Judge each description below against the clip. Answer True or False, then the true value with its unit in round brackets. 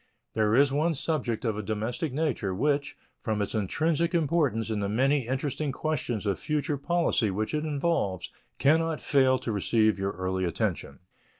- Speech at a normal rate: True (170 wpm)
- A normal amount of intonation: False (6.0 semitones)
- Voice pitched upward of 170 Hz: False (130 Hz)